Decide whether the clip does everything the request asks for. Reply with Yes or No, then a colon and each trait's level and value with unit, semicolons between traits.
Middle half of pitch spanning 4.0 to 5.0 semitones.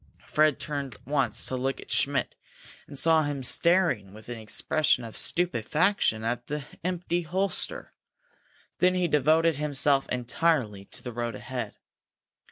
No: wide, 5.4 semitones